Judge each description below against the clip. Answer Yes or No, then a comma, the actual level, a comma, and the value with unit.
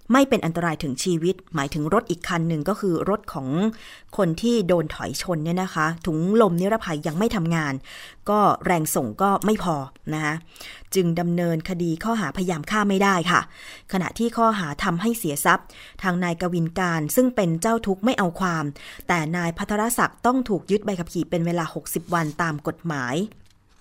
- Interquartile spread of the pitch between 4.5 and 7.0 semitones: No, average, 3.7 semitones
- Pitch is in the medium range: Yes, medium, 175 Hz